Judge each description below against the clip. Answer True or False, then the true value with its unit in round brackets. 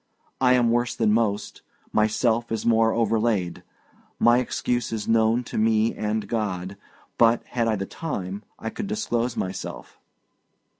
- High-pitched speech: False (115 Hz)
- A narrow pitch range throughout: True (1.8 semitones)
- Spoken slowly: False (145 wpm)